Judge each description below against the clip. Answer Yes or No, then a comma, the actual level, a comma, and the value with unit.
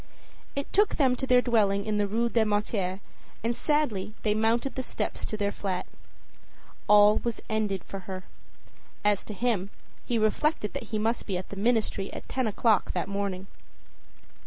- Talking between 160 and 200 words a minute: Yes, average, 175 wpm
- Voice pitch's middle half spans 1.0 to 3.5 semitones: Yes, average, 3.0 semitones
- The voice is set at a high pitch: Yes, high, 215 Hz